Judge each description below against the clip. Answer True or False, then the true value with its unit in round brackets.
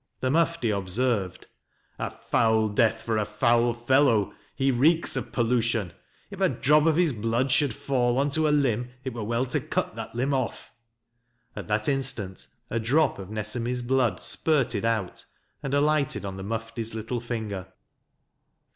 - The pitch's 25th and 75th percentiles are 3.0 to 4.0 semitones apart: True (3.7 semitones)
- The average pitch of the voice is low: True (120 Hz)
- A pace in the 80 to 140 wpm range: False (165 wpm)